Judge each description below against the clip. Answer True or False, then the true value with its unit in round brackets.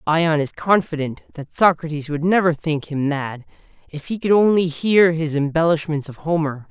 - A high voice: False (160 Hz)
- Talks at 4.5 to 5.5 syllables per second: True (4.8 syllables/s)